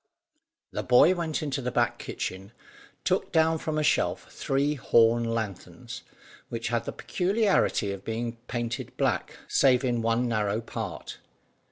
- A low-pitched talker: Yes, low, 120 Hz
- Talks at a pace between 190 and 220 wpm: No, average, 145 wpm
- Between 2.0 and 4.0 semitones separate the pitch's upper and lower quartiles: No, average, 4.5 semitones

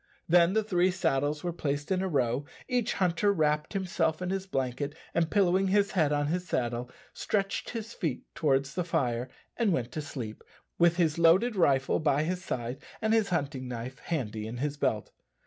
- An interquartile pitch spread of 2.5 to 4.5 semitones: No, wide, 5.5 semitones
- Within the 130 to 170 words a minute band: No, average, 185 wpm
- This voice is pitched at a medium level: Yes, medium, 160 Hz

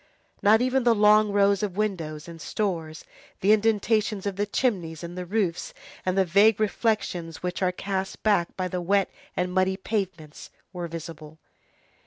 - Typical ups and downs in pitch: Yes, average, 3.4 semitones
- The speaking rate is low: No, average, 165 wpm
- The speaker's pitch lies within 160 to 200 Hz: Yes, high, 190 Hz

